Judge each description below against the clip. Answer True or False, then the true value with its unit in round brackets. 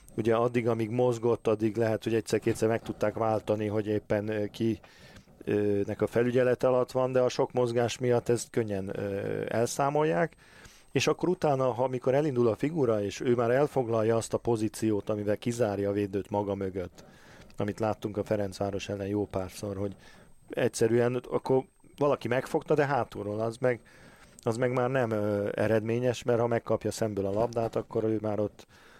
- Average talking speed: False (165 wpm)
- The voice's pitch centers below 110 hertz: False (115 Hz)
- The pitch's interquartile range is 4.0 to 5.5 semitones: False (2.9 semitones)